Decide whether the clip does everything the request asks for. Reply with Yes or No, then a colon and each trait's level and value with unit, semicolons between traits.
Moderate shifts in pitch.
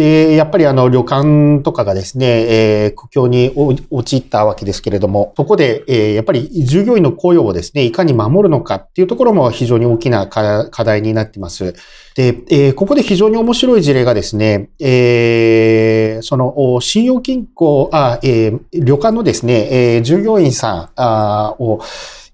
No: wide, 5.9 semitones